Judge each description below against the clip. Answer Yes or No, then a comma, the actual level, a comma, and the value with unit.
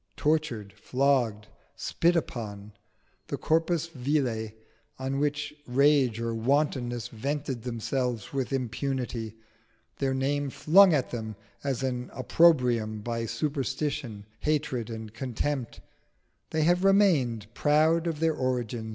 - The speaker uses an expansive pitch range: No, average, 4.3 semitones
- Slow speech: Yes, slow, 115 wpm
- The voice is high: No, low, 130 Hz